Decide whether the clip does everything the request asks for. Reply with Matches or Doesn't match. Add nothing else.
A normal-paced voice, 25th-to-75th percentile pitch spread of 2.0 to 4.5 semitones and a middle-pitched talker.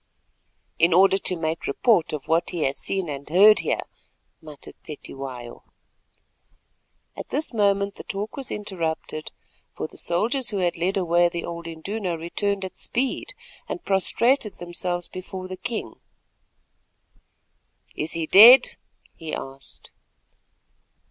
Doesn't match